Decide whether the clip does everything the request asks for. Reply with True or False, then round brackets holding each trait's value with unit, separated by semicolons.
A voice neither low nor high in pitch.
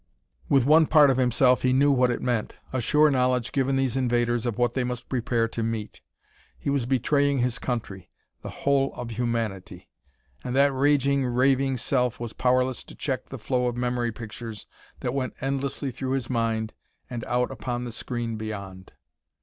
False (125 Hz)